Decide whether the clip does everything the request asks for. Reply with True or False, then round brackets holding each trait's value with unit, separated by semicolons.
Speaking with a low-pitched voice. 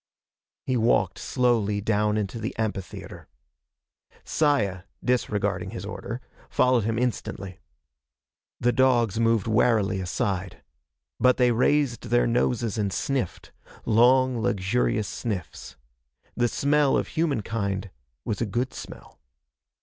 True (115 Hz)